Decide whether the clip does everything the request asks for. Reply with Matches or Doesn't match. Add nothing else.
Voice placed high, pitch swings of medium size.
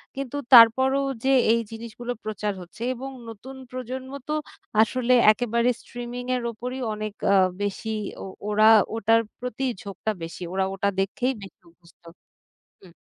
Matches